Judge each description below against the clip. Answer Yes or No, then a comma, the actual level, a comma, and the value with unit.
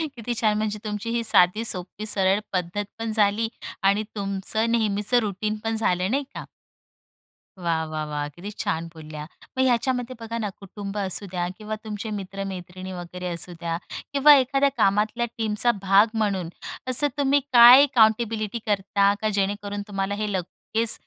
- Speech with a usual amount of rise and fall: Yes, average, 3.0 semitones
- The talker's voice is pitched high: Yes, high, 210 Hz